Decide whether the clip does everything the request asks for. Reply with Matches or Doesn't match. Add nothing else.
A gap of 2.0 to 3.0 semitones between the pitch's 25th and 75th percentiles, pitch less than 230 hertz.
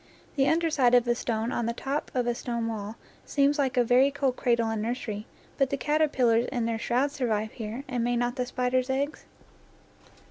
Doesn't match